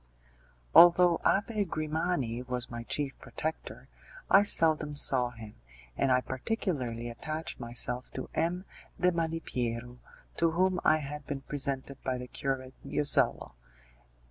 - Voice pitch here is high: No, medium, 145 Hz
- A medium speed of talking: No, slow, 125 wpm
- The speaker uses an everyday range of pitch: Yes, average, 4.8 semitones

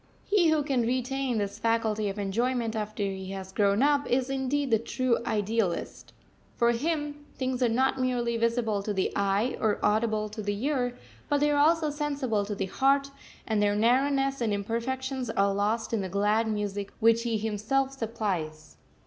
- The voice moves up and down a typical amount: Yes, average, 4.2 semitones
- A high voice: Yes, high, 230 Hz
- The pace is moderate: Yes, average, 175 wpm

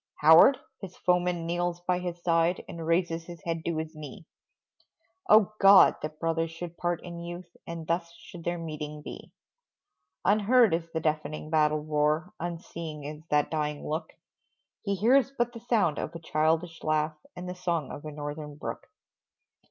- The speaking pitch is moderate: Yes, medium, 165 Hz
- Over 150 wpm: Yes, average, 165 wpm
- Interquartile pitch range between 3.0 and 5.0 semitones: No, narrow, 2.4 semitones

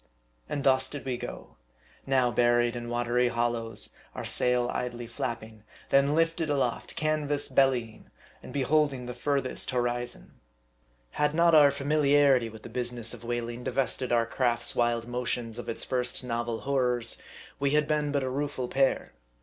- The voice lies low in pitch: Yes, low, 125 Hz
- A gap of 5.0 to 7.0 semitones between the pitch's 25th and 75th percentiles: No, average, 2.8 semitones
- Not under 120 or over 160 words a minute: Yes, average, 155 wpm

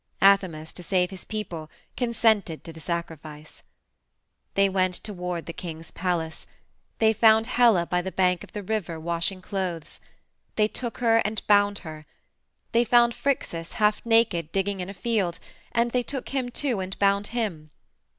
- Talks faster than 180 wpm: No, average, 160 wpm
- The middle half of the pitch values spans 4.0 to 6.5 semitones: Yes, average, 4.5 semitones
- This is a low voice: No, high, 195 Hz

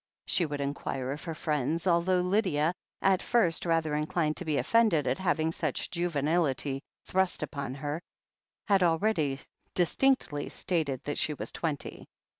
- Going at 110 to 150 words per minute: Yes, average, 145 wpm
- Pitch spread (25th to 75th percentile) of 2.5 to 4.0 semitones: Yes, average, 3.6 semitones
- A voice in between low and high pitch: Yes, medium, 160 Hz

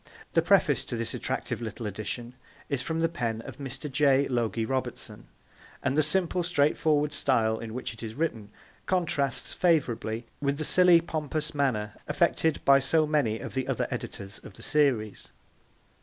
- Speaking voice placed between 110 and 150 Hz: Yes, medium, 140 Hz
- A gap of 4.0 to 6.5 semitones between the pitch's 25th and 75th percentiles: Yes, average, 5.1 semitones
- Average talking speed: Yes, average, 165 wpm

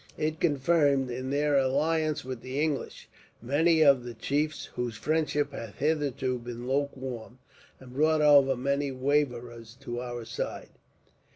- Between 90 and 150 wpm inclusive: Yes, slow, 135 wpm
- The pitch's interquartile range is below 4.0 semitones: Yes, average, 3.3 semitones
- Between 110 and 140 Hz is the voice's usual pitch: Yes, low, 135 Hz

